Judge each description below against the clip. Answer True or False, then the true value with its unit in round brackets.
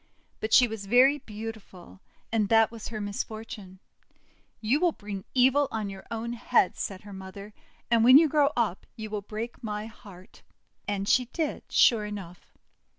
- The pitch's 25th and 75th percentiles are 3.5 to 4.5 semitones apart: False (2.9 semitones)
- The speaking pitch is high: True (220 Hz)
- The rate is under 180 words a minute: True (165 wpm)